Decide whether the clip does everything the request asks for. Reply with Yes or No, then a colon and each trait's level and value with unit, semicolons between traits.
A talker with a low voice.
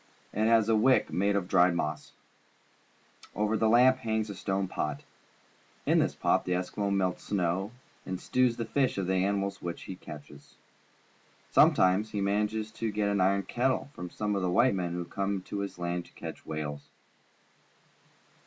Yes: low, 100 Hz